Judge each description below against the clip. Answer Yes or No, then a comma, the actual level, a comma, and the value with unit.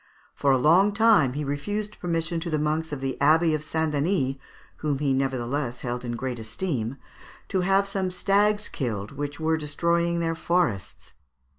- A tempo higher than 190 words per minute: No, average, 170 wpm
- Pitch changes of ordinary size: Yes, average, 4.6 semitones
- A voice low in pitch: No, medium, 155 Hz